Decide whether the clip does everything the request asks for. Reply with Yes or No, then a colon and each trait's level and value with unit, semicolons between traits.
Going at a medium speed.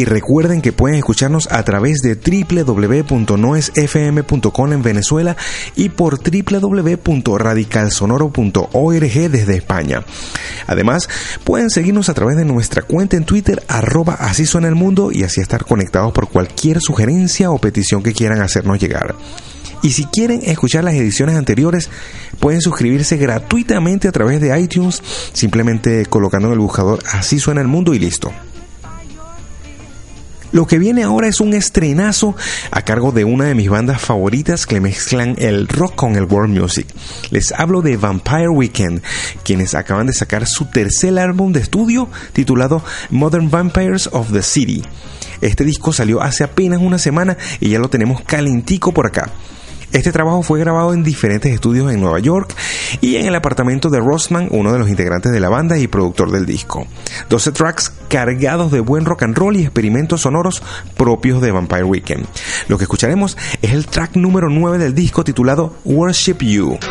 Yes: average, 160 wpm